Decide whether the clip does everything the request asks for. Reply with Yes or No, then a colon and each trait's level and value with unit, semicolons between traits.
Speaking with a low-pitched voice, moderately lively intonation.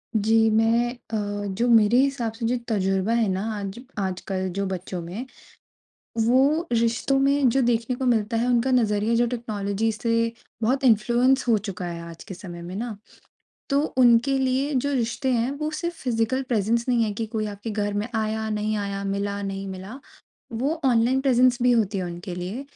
No: high, 225 Hz; average, 3.5 semitones